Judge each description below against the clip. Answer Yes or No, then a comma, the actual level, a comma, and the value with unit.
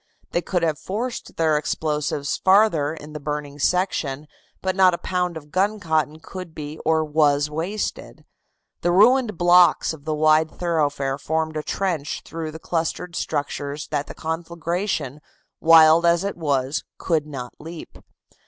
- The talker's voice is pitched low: No, medium, 160 Hz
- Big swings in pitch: No, average, 2.8 semitones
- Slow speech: No, average, 150 wpm